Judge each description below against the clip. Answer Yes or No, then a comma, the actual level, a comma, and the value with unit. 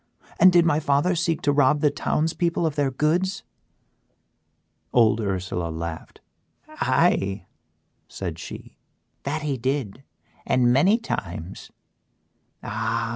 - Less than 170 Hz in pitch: Yes, medium, 140 Hz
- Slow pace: Yes, slow, 120 wpm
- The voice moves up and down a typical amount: No, wide, 6.3 semitones